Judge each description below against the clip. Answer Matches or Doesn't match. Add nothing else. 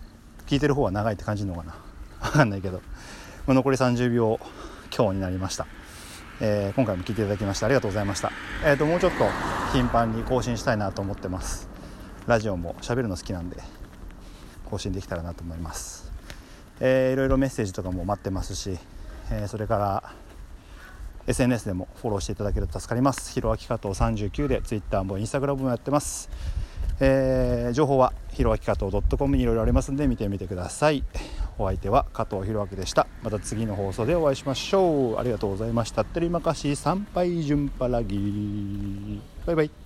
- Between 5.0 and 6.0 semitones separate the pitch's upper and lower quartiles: Matches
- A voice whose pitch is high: Doesn't match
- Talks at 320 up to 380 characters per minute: Doesn't match